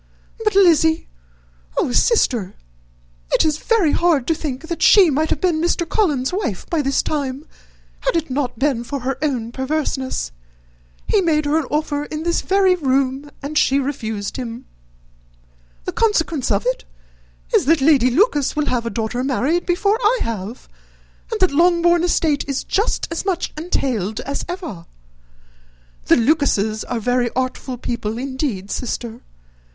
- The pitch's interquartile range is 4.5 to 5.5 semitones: Yes, average, 5.1 semitones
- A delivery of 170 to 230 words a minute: No, average, 155 wpm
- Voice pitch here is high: Yes, very high, 285 Hz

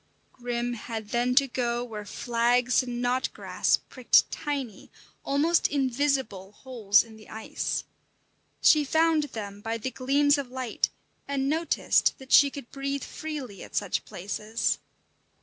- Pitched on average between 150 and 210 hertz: No, very high, 250 Hz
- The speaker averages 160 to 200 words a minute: No, slow, 135 wpm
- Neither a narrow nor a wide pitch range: Yes, average, 3.6 semitones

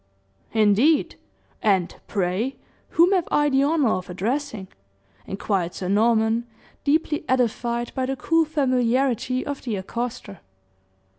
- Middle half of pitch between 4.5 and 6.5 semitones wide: Yes, average, 5.2 semitones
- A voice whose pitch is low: No, high, 240 Hz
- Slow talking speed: Yes, slow, 120 wpm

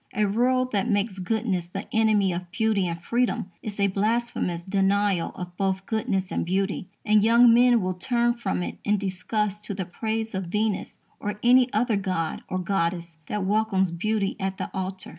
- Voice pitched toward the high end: Yes, high, 200 Hz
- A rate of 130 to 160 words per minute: No, average, 180 wpm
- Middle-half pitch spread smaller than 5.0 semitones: Yes, average, 2.9 semitones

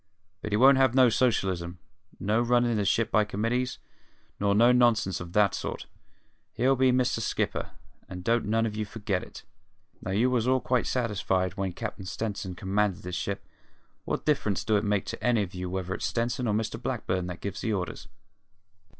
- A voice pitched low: Yes, low, 105 Hz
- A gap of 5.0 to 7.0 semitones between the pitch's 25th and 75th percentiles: No, average, 4.1 semitones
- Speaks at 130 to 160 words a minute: No, average, 190 wpm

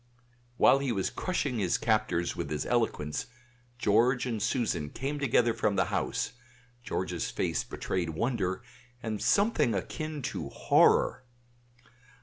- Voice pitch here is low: Yes, low, 115 Hz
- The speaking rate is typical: No, slow, 130 wpm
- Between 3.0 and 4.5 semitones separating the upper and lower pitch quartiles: No, average, 5.3 semitones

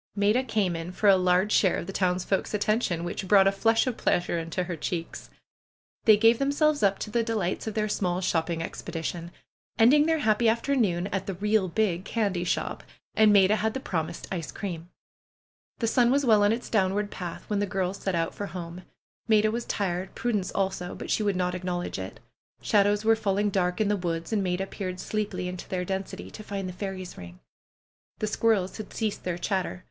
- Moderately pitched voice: No, high, 195 Hz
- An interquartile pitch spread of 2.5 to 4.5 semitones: Yes, average, 3.2 semitones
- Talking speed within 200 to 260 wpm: Yes, fast, 205 wpm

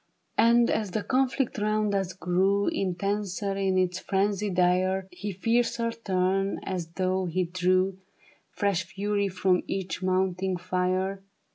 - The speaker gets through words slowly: Yes, slow, 130 wpm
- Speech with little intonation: Yes, narrow, 1.7 semitones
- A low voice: No, high, 190 Hz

